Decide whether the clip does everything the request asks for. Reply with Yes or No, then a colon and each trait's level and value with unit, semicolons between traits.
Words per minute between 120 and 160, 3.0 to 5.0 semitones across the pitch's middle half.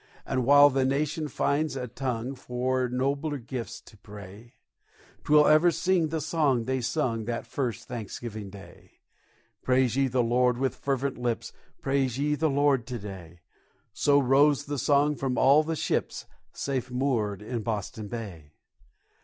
Yes: average, 155 wpm; average, 3.5 semitones